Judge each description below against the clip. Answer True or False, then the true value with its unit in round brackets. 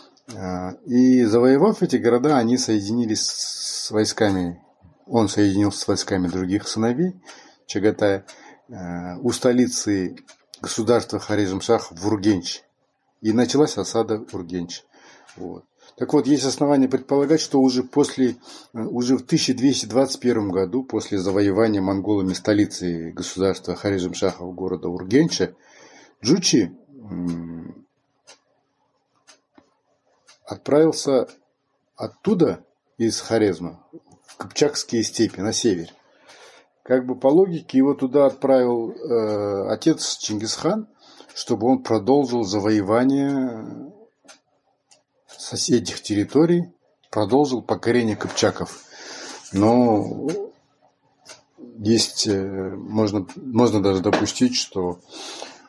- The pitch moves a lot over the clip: False (4.7 semitones)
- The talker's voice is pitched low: True (110 Hz)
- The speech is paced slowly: True (90 wpm)